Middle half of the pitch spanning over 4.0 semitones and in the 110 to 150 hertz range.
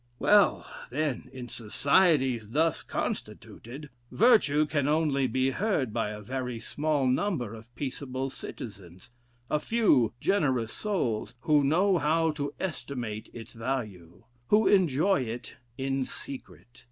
Yes: average, 4.8 semitones; low, 135 Hz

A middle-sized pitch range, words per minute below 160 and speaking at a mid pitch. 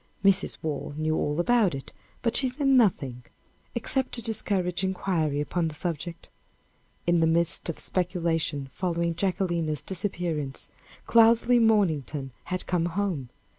Yes: average, 4.2 semitones; slow, 135 wpm; medium, 175 Hz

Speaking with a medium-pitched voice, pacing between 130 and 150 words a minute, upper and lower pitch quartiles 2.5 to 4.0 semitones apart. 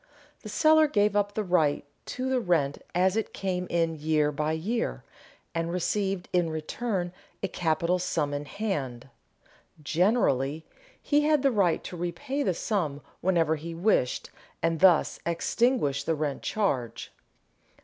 No: medium, 175 Hz; average, 145 wpm; average, 4.9 semitones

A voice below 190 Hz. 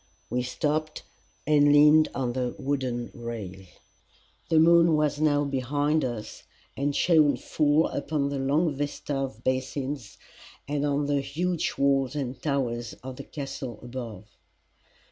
Yes: medium, 140 Hz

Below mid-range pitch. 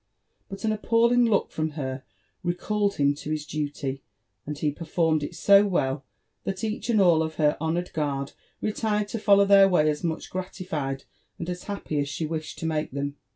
No: medium, 165 Hz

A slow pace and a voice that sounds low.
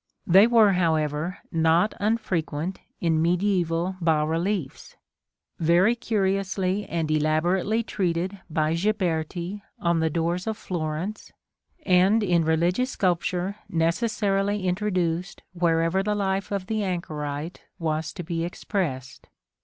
No: slow, 115 wpm; medium, 180 Hz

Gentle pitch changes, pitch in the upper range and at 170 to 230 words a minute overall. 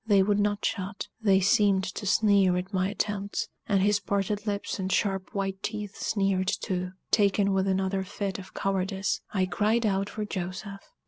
Yes: narrow, 1.3 semitones; high, 195 Hz; average, 175 wpm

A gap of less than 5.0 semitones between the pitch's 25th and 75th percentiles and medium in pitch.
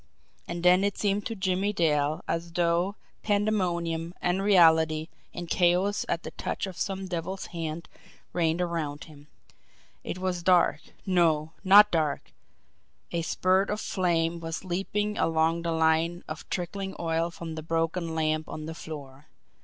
Yes: narrow, 2.6 semitones; medium, 170 Hz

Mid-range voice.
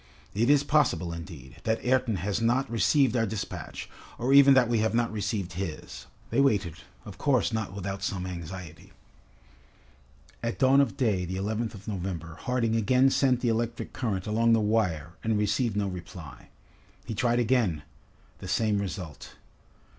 No: low, 110 Hz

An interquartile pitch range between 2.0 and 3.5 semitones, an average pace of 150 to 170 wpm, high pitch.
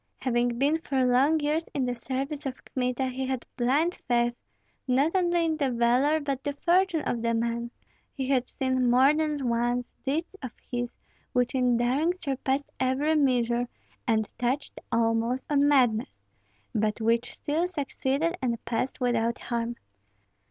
Yes: average, 3.2 semitones; average, 155 wpm; very high, 260 Hz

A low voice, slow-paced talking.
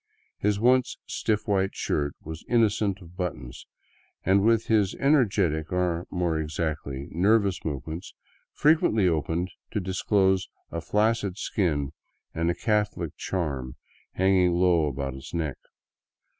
Yes: very low, 90 Hz; slow, 130 wpm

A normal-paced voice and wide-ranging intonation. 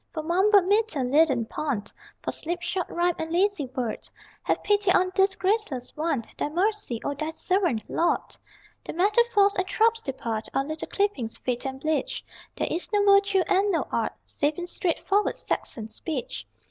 Yes: average, 165 wpm; wide, 6.4 semitones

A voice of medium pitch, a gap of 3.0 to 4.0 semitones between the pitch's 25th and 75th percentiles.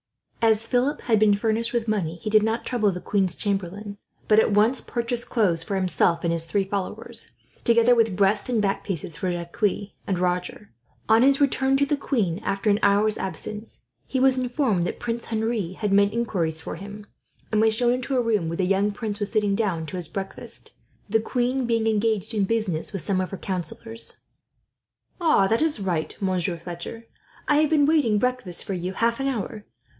No: high, 210 Hz; average, 3.5 semitones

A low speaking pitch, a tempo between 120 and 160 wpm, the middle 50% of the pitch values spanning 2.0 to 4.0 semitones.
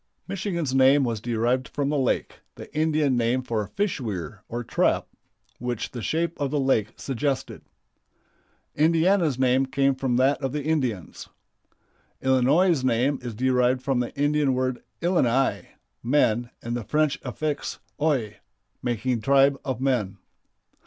Yes: low, 130 Hz; average, 140 wpm; average, 3.2 semitones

